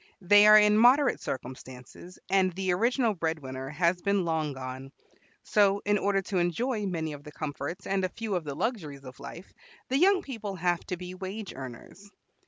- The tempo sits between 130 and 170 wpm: No, average, 185 wpm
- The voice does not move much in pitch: No, average, 5.3 semitones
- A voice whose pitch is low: No, medium, 185 Hz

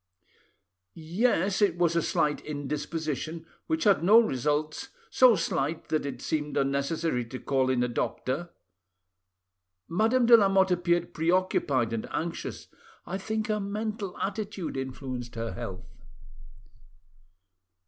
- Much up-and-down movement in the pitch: Yes, wide, 6.1 semitones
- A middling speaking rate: No, slow, 120 wpm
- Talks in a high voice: No, medium, 165 Hz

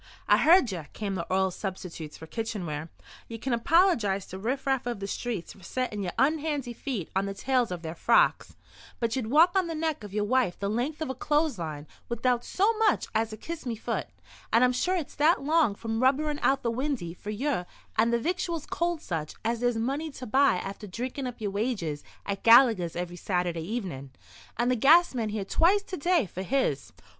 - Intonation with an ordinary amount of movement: No, wide, 6.5 semitones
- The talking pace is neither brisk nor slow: No, fast, 210 wpm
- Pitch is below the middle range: No, high, 235 Hz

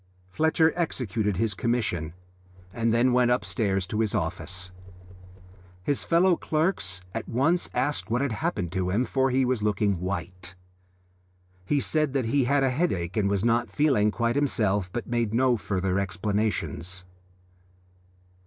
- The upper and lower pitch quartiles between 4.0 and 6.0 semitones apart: Yes, wide, 5.5 semitones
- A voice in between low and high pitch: No, low, 115 Hz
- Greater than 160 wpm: No, average, 145 wpm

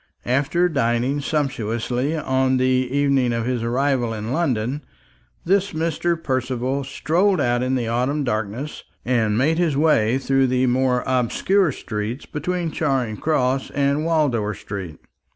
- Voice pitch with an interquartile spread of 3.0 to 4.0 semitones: Yes, average, 3.6 semitones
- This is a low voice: Yes, low, 130 Hz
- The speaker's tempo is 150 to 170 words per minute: No, slow, 135 wpm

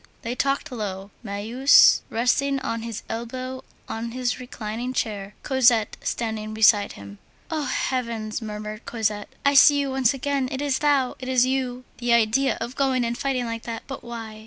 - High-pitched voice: Yes, high, 240 Hz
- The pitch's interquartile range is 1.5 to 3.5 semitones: Yes, average, 3.1 semitones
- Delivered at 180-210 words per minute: No, average, 170 wpm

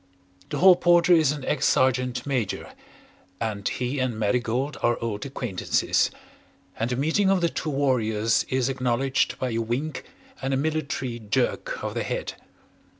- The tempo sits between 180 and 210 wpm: No, average, 155 wpm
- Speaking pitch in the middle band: No, low, 130 Hz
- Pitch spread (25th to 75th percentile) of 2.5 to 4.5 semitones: Yes, average, 3.7 semitones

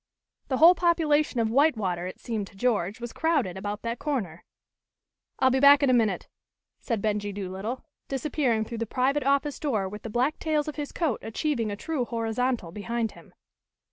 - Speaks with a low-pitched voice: No, high, 240 Hz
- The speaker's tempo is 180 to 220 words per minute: Yes, average, 185 wpm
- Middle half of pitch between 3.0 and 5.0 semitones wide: No, wide, 5.4 semitones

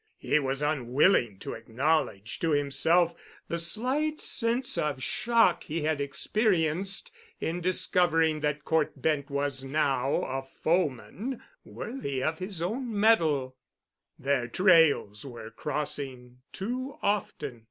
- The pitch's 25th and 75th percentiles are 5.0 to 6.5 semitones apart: Yes, wide, 5.6 semitones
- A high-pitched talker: No, medium, 155 Hz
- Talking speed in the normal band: No, slow, 120 wpm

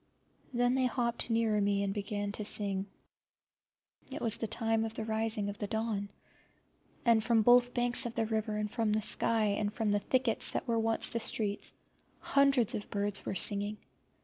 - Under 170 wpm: No, average, 185 wpm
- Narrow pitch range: Yes, narrow, 2.2 semitones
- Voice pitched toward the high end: Yes, high, 220 Hz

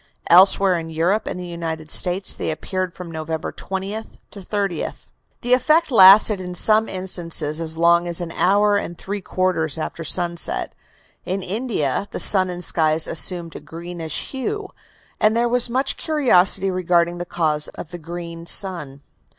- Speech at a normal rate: Yes, average, 160 wpm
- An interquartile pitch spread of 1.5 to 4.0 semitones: Yes, average, 3.2 semitones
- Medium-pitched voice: Yes, medium, 180 Hz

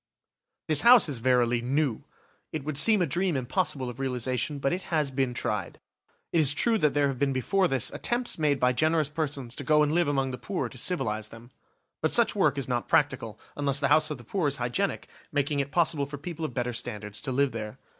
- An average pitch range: Yes, average, 3.7 semitones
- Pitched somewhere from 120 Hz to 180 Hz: Yes, medium, 140 Hz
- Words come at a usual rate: No, fast, 225 wpm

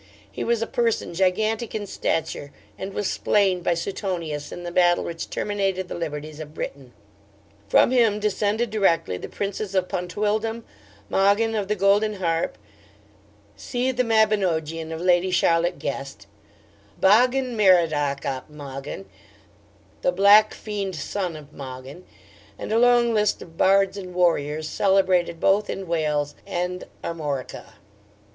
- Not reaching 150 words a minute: Yes, average, 140 wpm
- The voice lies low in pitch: No, medium, 185 Hz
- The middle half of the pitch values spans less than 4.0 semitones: No, average, 4.4 semitones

